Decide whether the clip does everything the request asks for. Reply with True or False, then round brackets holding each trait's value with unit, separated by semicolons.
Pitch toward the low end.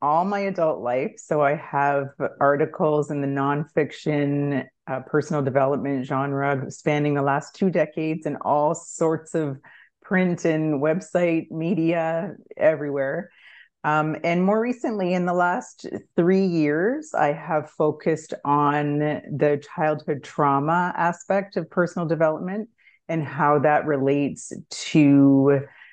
False (155 Hz)